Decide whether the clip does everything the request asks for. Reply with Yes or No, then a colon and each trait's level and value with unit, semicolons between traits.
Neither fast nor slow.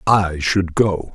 Yes: average, 155 wpm